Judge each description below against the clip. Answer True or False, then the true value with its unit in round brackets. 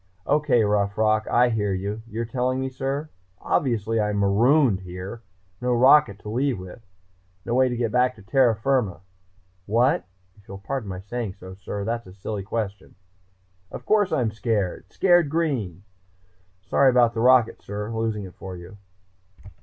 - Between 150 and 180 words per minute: True (165 wpm)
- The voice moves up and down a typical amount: True (4.1 semitones)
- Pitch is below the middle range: True (115 Hz)